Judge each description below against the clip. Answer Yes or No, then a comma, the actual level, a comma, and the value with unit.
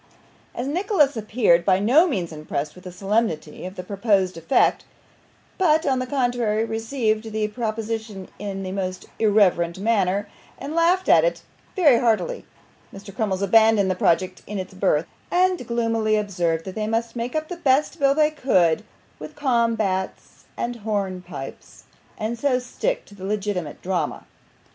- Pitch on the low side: No, high, 215 Hz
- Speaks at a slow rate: No, average, 155 wpm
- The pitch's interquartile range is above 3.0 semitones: Yes, average, 4.7 semitones